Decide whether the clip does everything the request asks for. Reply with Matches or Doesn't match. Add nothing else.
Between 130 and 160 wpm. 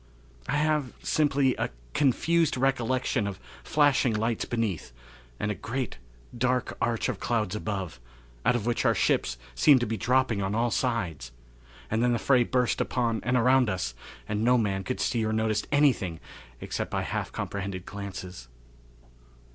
Matches